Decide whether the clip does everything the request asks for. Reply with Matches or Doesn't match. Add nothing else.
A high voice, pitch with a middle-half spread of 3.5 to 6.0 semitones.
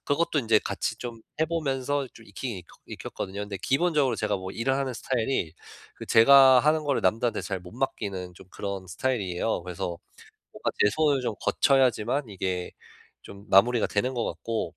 Doesn't match